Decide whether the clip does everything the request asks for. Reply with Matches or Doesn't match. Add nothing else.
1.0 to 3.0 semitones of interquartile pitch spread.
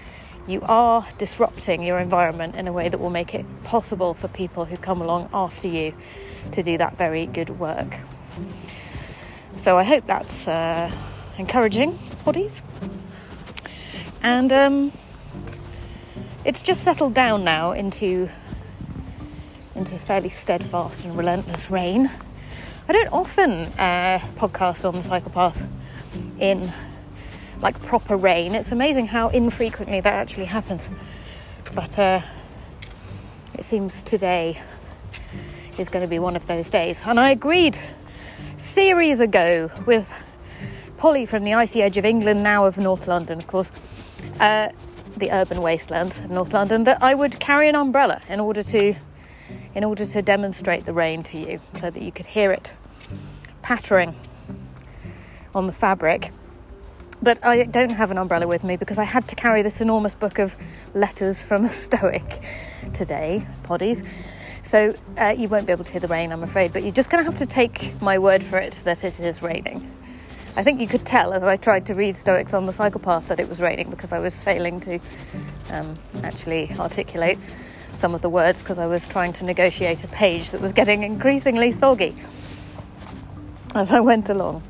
Doesn't match